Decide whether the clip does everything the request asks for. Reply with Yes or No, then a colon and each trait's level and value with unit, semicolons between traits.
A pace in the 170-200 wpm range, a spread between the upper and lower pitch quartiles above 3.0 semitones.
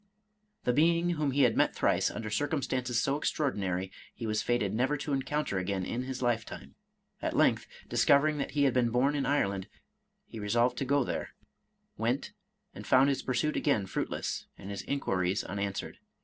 Yes: average, 180 wpm; wide, 5.5 semitones